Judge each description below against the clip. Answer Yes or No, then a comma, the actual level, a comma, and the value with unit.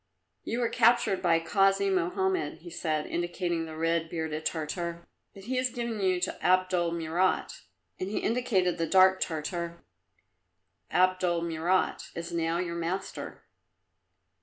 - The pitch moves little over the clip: Yes, narrow, 2.3 semitones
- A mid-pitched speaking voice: Yes, medium, 175 Hz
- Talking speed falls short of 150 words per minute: Yes, slow, 135 wpm